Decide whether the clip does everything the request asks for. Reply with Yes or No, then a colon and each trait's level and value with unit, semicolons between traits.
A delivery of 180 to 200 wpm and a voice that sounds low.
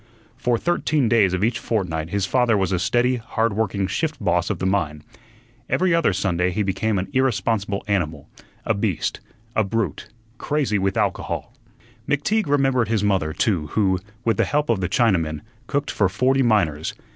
No: average, 170 wpm; low, 105 Hz